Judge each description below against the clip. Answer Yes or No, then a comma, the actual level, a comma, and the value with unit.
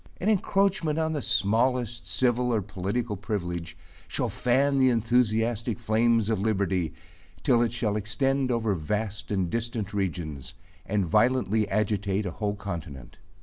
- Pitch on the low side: Yes, low, 110 Hz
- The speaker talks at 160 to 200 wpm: No, average, 140 wpm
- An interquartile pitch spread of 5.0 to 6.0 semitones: No, average, 3.6 semitones